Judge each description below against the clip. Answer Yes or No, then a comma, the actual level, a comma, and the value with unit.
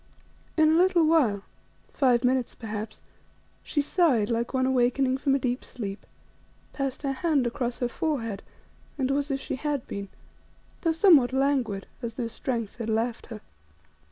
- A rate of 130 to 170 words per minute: Yes, average, 155 wpm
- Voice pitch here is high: Yes, very high, 255 Hz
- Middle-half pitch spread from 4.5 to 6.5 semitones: No, average, 3.6 semitones